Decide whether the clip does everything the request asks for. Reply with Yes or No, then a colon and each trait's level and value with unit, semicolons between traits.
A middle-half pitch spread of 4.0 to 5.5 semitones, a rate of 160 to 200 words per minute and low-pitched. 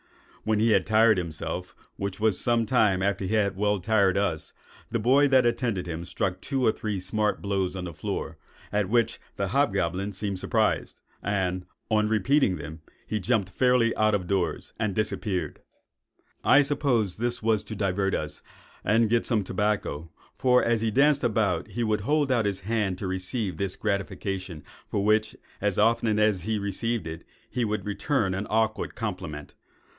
No: average, 3.4 semitones; average, 175 wpm; low, 105 Hz